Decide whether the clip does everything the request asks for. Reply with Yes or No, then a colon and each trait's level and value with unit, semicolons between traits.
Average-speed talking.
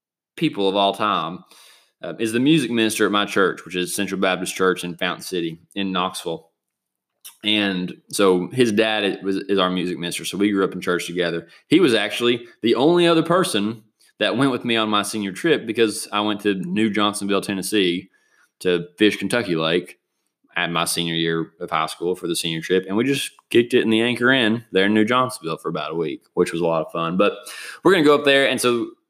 No: fast, 220 wpm